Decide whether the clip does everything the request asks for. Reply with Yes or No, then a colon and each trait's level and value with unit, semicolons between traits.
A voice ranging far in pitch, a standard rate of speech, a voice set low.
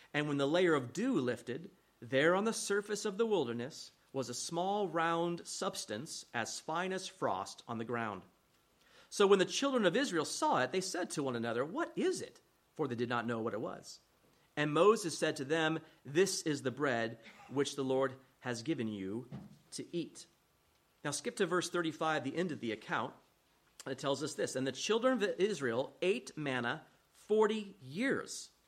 No: wide, 6.8 semitones; average, 190 wpm; medium, 160 Hz